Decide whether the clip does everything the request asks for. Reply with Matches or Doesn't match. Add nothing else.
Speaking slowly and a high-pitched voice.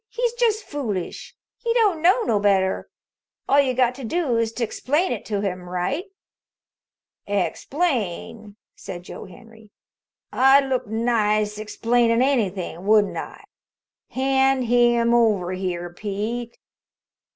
Matches